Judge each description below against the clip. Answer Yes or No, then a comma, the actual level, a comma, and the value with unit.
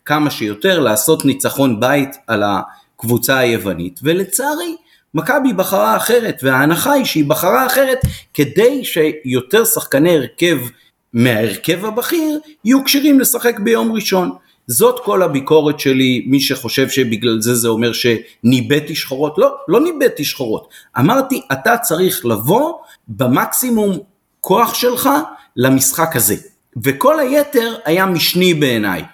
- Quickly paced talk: No, average, 120 wpm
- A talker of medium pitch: Yes, medium, 165 Hz